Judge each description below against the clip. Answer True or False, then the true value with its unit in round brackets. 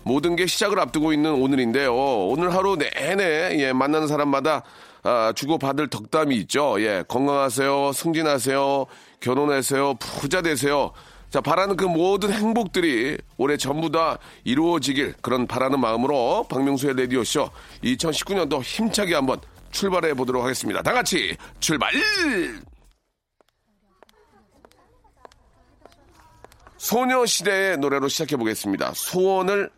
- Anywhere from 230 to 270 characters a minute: False (285 characters per minute)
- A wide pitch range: True (5.8 semitones)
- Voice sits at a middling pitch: True (150 Hz)